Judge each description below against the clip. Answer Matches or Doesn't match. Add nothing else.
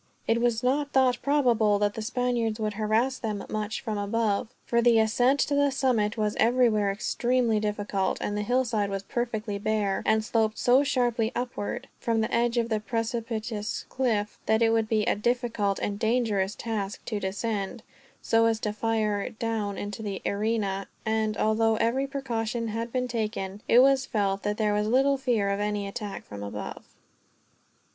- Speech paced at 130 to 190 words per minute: Matches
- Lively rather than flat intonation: Doesn't match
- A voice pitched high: Matches